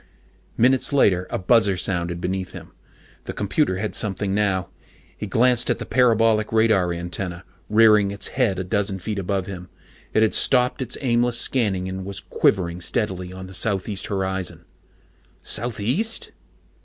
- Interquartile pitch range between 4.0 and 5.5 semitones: No, average, 3.5 semitones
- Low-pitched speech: Yes, low, 100 Hz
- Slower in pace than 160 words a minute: Yes, average, 150 wpm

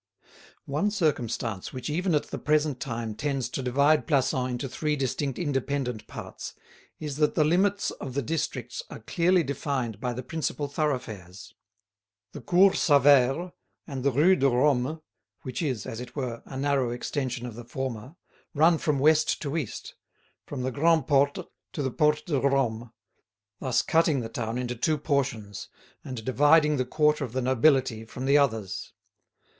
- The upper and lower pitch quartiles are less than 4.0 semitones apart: Yes, average, 3.5 semitones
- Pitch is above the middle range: No, low, 135 Hz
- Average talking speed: Yes, average, 165 wpm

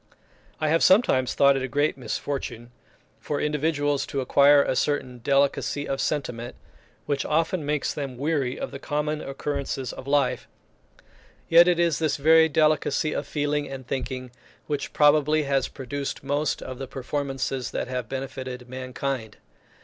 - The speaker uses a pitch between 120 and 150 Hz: Yes, medium, 140 Hz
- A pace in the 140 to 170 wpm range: Yes, average, 150 wpm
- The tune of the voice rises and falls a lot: No, narrow, 2.4 semitones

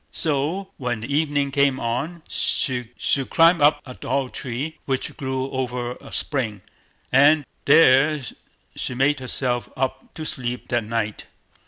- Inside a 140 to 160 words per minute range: Yes, average, 145 wpm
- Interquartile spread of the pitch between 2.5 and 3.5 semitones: Yes, average, 2.9 semitones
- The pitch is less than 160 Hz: Yes, low, 135 Hz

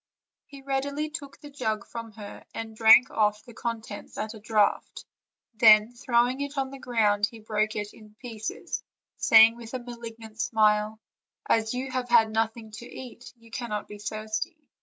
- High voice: Yes, high, 225 Hz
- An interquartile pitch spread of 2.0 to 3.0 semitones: Yes, narrow, 2.4 semitones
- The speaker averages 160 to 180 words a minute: Yes, average, 170 wpm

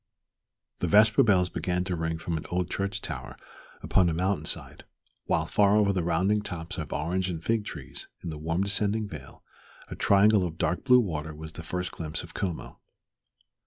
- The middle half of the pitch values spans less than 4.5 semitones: Yes, average, 3.5 semitones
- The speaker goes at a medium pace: Yes, average, 190 wpm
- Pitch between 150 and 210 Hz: No, very low, 90 Hz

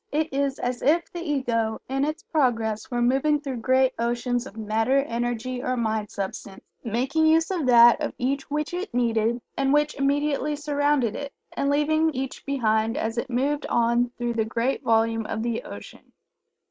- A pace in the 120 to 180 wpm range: Yes, average, 175 wpm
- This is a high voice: Yes, very high, 255 Hz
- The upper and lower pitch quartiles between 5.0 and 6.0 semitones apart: No, average, 3.8 semitones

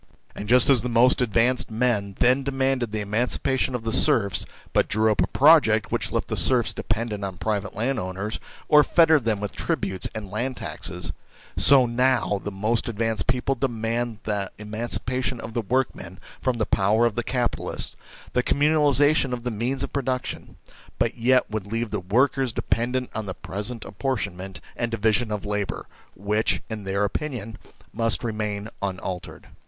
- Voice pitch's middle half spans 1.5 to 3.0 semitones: No, average, 3.5 semitones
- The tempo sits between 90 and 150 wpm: No, average, 170 wpm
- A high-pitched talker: No, low, 115 Hz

